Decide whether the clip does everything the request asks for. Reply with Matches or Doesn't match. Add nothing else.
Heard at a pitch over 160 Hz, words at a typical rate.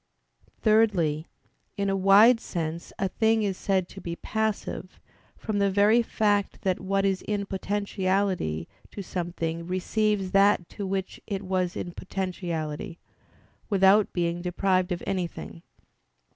Doesn't match